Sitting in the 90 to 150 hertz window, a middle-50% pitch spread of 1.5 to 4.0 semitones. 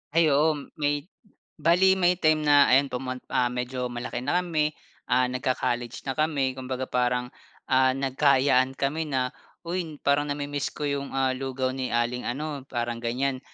Yes: low, 135 Hz; narrow, 2.5 semitones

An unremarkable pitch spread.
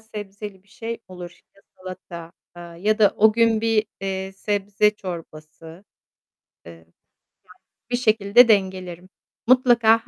Yes: average, 3.4 semitones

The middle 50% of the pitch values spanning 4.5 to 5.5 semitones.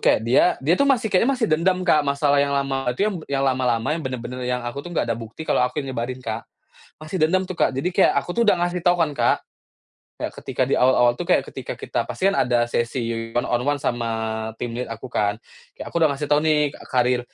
Yes: average, 4.8 semitones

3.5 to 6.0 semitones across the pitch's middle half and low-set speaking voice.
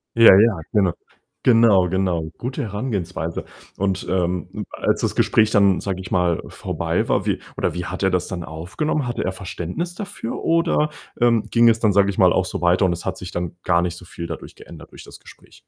Yes: average, 4.2 semitones; very low, 95 Hz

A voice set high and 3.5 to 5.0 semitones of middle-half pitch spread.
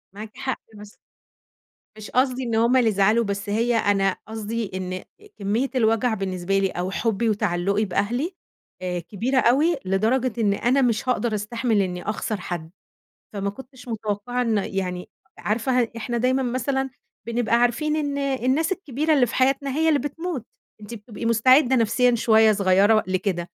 Yes: high, 225 Hz; average, 4.1 semitones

